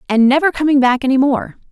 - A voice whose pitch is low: No, very high, 260 Hz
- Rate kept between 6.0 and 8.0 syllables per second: Yes, 6.3 syllables/s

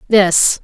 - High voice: Yes, high, 195 Hz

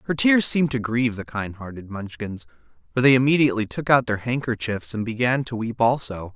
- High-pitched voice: No, low, 115 Hz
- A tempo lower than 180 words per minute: No, average, 200 wpm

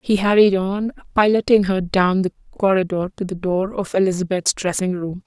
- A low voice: No, high, 190 Hz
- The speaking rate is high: No, average, 170 wpm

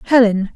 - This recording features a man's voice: No, female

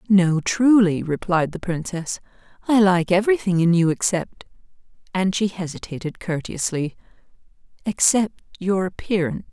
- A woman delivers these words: Yes, female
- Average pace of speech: No, slow, 100 wpm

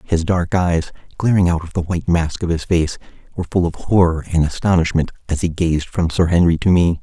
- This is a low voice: Yes, very low, 85 Hz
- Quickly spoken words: Yes, fast, 220 wpm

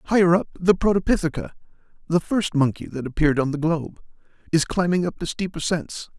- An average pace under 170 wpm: Yes, average, 155 wpm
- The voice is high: No, medium, 170 Hz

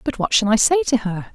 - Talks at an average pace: No, fast, 310 wpm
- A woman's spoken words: Yes, female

